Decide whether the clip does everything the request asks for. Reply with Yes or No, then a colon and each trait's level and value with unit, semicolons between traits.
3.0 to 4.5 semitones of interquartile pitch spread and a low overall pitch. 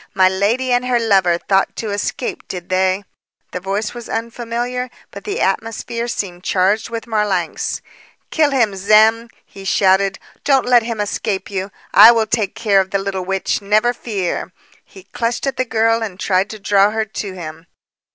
No: average, 3.3 semitones; high, 210 Hz